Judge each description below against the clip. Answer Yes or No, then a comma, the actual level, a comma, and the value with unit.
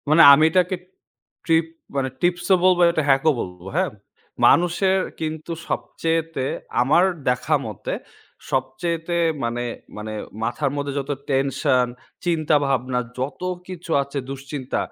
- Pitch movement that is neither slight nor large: Yes, average, 4.2 semitones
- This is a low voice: No, medium, 145 Hz